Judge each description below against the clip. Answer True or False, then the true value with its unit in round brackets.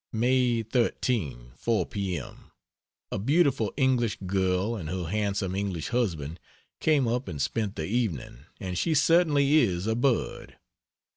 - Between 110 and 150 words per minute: True (140 wpm)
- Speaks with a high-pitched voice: False (105 Hz)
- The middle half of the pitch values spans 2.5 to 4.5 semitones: False (5.5 semitones)